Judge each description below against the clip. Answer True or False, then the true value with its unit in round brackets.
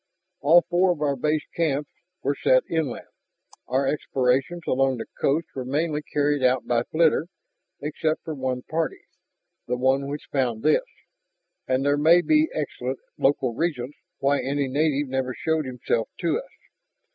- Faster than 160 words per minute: False (155 wpm)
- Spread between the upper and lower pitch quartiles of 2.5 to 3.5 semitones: True (3.2 semitones)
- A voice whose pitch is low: False (145 Hz)